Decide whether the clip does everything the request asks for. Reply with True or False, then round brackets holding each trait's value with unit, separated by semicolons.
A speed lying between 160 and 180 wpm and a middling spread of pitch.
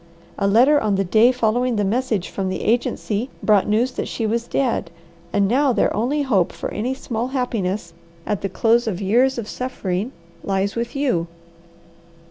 True (175 wpm; 3.9 semitones)